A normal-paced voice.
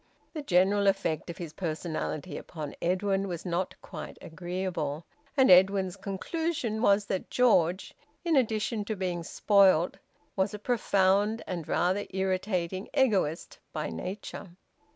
No: slow, 130 wpm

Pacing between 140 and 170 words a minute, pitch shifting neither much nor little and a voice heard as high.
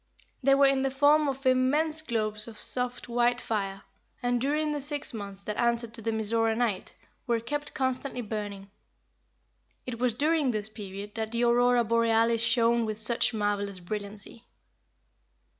Yes: average, 160 wpm; average, 3.3 semitones; high, 235 Hz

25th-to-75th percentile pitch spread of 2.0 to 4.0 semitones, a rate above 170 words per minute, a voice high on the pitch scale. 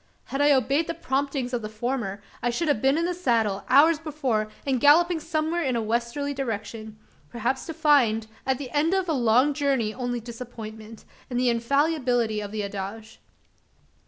No: average, 4.6 semitones; average, 180 wpm; very high, 250 Hz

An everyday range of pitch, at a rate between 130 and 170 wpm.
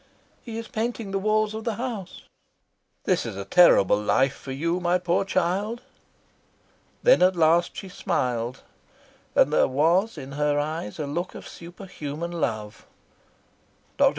No: wide, 5.7 semitones; average, 150 wpm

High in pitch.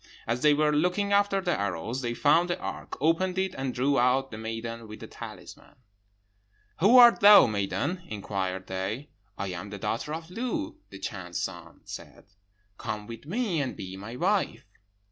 No: low, 135 Hz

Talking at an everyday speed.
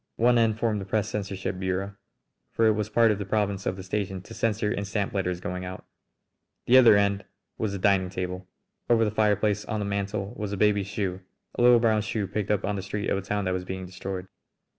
No: fast, 230 wpm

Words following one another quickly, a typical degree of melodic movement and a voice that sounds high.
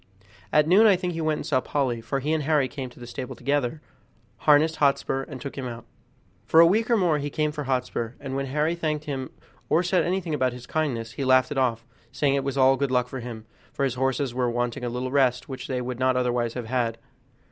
No: fast, 245 wpm; average, 3.3 semitones; low, 135 Hz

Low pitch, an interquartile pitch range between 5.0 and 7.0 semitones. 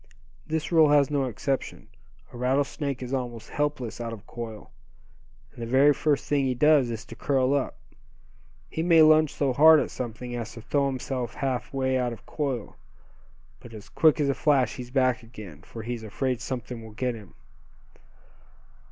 No: low, 130 Hz; average, 3.3 semitones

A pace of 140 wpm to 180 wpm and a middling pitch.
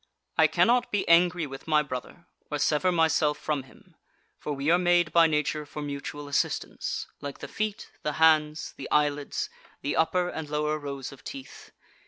Yes: average, 175 wpm; medium, 150 Hz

